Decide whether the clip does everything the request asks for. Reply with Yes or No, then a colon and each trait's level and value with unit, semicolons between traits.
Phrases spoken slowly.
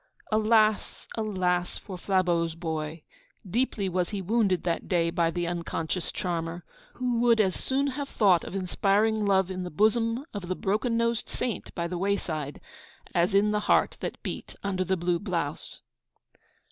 No: average, 160 wpm